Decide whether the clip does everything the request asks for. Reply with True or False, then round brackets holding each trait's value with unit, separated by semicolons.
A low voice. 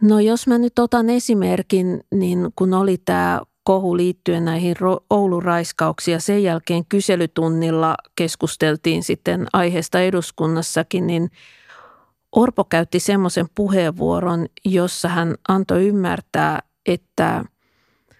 False (180 Hz)